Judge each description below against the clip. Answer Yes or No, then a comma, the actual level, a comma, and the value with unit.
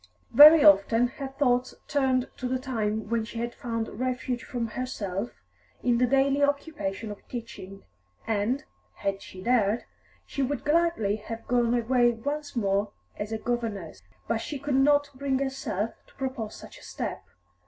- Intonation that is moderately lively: Yes, average, 3.6 semitones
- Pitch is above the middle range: Yes, high, 245 Hz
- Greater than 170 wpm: No, average, 160 wpm